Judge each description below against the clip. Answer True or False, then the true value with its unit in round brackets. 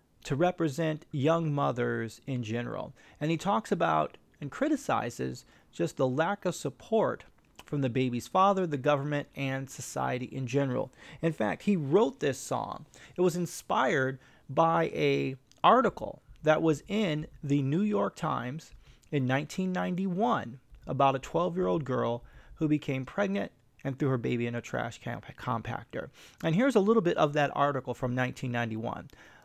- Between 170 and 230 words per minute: False (155 wpm)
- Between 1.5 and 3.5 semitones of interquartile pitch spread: False (4.5 semitones)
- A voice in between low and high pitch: True (145 Hz)